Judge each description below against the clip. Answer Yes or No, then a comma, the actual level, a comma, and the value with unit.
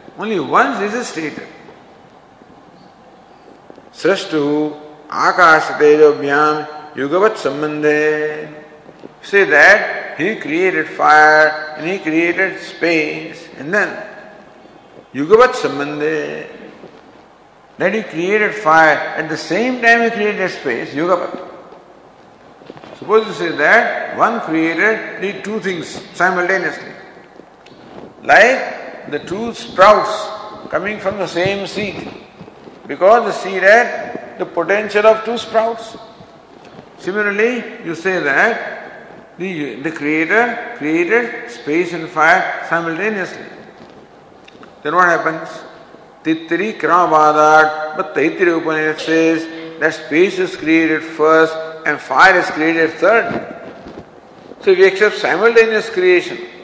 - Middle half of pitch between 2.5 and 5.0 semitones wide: No, wide, 5.5 semitones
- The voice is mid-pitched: Yes, medium, 180 Hz